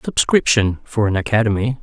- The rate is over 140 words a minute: No, slow, 130 wpm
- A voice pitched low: Yes, low, 110 Hz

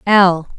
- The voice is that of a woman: Yes, female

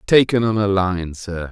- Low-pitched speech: Yes, low, 100 Hz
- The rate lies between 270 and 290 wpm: No, average, 200 wpm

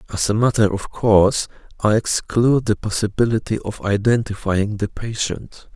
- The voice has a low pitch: Yes, low, 105 Hz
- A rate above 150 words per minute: No, slow, 135 wpm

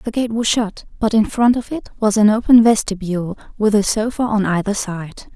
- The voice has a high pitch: Yes, high, 215 Hz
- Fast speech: Yes, fast, 215 wpm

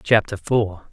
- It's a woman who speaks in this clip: No, male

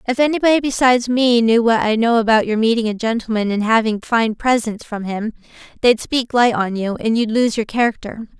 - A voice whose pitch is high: Yes, high, 230 Hz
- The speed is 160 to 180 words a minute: No, fast, 205 wpm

